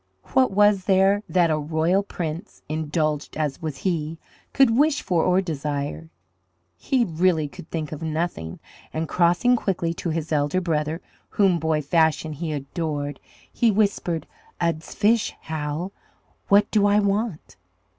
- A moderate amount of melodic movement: Yes, average, 4.2 semitones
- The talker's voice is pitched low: No, medium, 165 Hz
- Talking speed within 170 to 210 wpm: No, average, 145 wpm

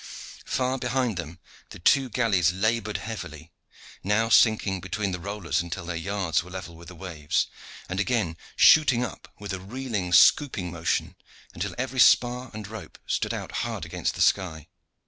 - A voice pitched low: Yes, low, 100 Hz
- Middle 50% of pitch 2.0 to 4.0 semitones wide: No, average, 5.1 semitones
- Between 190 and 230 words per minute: No, average, 165 wpm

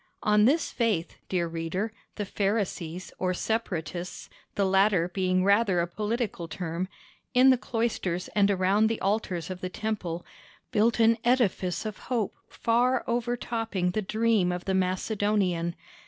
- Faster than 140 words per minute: No, slow, 135 wpm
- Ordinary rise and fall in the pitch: Yes, average, 3.9 semitones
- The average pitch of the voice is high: Yes, high, 200 Hz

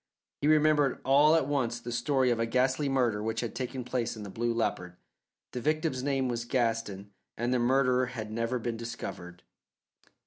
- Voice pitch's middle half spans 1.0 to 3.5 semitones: Yes, average, 2.8 semitones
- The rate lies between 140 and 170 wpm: No, average, 180 wpm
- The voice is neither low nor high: No, low, 125 Hz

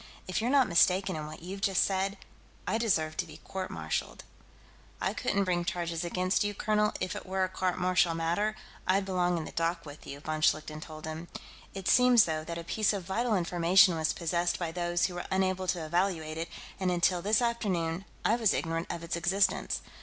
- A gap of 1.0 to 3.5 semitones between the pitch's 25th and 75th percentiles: Yes, average, 2.7 semitones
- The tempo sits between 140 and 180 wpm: No, fast, 205 wpm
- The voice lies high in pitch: No, medium, 180 Hz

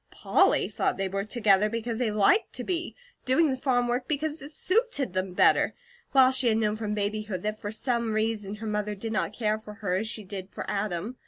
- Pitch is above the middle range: Yes, high, 215 Hz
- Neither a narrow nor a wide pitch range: Yes, average, 3.4 semitones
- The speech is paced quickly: Yes, fast, 220 wpm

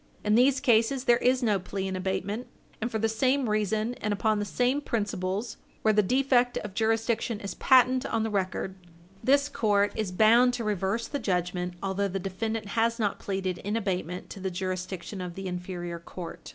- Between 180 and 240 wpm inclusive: Yes, average, 190 wpm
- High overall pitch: Yes, high, 210 Hz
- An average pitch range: Yes, average, 3.6 semitones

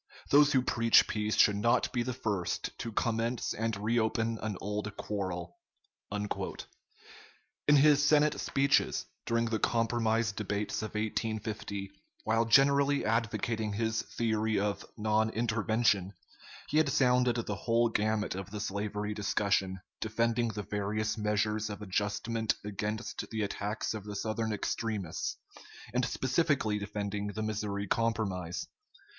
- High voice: No, low, 110 Hz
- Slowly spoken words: Yes, slow, 130 wpm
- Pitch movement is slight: Yes, narrow, 2.0 semitones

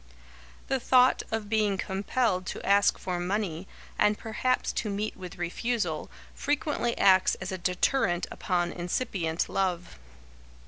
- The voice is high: Yes, high, 195 Hz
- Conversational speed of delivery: No, slow, 130 wpm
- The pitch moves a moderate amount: Yes, average, 3.8 semitones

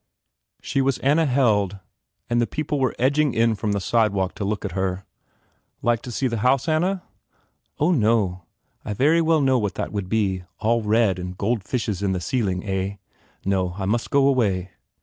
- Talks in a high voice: No, low, 110 Hz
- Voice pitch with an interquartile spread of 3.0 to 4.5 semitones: No, average, 5.2 semitones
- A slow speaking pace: No, average, 190 wpm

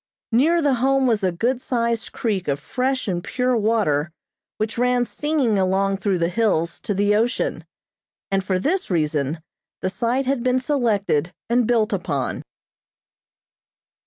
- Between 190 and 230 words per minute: No, average, 150 wpm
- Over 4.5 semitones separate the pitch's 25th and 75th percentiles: Yes, average, 5.1 semitones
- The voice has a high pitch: Yes, high, 220 Hz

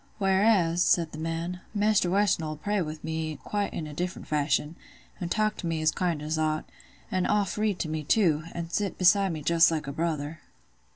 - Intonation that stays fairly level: No, average, 3.6 semitones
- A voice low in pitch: No, medium, 170 Hz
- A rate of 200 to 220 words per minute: Yes, fast, 205 wpm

